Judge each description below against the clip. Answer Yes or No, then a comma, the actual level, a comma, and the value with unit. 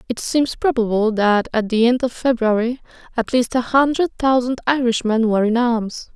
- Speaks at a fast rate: No, average, 175 wpm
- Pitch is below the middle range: No, high, 240 Hz